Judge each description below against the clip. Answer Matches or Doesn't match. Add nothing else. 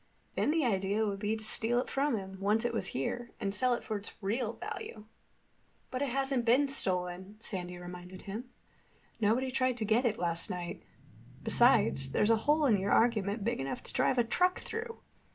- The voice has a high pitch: Matches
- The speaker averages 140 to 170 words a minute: Doesn't match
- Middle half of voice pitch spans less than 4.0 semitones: Doesn't match